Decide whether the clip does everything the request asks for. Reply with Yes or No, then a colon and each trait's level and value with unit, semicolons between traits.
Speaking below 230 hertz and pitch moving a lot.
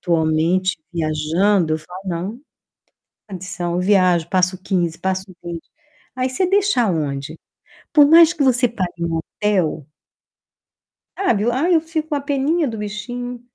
Yes: high, 190 Hz; wide, 7.2 semitones